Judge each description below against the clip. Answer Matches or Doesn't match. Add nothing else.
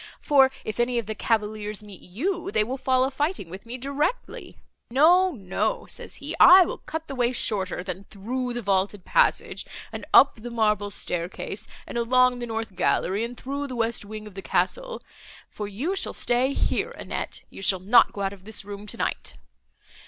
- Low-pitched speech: Doesn't match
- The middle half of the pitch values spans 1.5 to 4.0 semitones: Doesn't match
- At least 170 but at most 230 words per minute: Matches